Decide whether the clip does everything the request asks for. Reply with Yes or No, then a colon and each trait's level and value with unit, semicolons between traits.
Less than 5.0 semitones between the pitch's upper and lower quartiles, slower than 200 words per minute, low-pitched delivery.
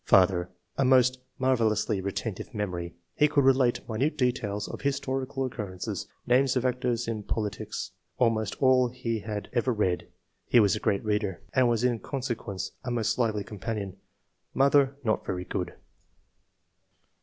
Yes: average, 3.9 semitones; average, 160 wpm; low, 115 Hz